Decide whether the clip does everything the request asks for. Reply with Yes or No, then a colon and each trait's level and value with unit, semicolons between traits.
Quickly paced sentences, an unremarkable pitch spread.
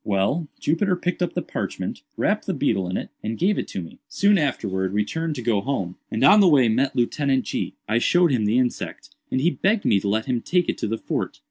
No: fast, 245 wpm; wide, 8.1 semitones